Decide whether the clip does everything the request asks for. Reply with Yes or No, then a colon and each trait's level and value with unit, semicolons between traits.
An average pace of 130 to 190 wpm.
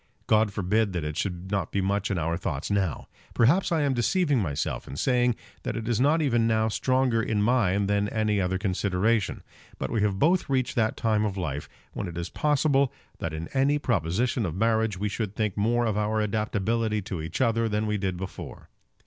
No: fast, 205 wpm